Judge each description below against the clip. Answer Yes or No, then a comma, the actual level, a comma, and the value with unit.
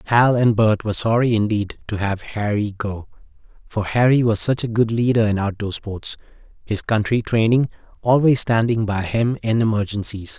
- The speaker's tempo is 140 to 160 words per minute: No, average, 170 wpm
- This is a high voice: No, low, 110 Hz